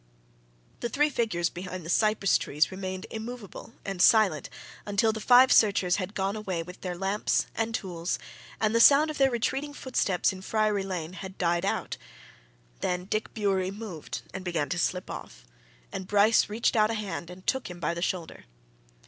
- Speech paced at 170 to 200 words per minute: Yes, average, 180 wpm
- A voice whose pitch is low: No, high, 195 Hz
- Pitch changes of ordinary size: Yes, average, 3.5 semitones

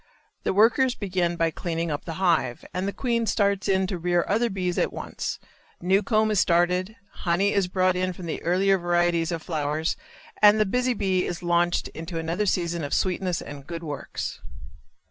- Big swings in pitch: No, narrow, 2.6 semitones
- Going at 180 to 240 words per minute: Yes, average, 185 wpm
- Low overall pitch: No, medium, 180 Hz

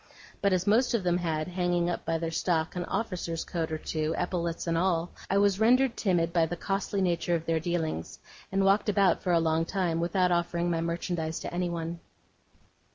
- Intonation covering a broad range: No, narrow, 2.4 semitones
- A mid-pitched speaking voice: Yes, medium, 175 Hz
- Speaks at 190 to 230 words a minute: Yes, average, 200 wpm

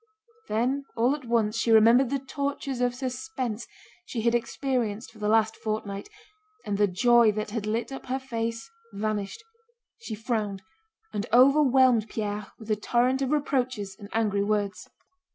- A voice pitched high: Yes, high, 230 Hz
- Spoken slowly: No, average, 155 wpm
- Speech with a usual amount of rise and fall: Yes, average, 3.3 semitones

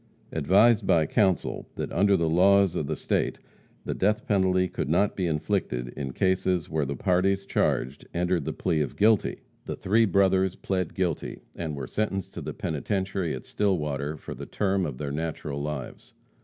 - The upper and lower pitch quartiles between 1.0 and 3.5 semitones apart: No, average, 4.4 semitones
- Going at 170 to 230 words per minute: Yes, average, 175 wpm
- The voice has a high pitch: No, very low, 90 Hz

